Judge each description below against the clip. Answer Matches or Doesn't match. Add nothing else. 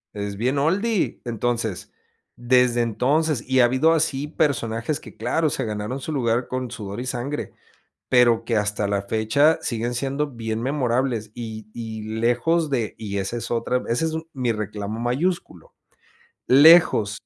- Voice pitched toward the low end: Matches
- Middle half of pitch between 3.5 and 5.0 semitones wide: Matches